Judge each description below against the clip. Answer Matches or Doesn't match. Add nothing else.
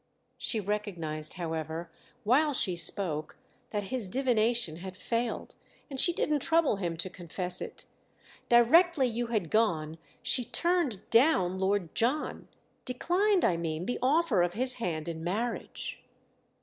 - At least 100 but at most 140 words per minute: Matches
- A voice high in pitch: Matches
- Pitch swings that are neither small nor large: Doesn't match